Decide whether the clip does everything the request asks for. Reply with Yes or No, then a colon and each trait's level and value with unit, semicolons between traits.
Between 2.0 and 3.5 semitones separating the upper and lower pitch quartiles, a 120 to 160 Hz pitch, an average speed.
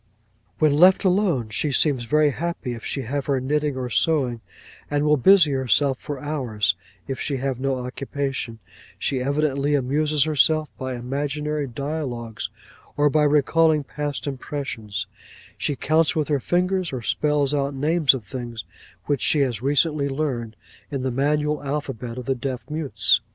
Yes: average, 2.9 semitones; medium, 140 Hz; average, 155 wpm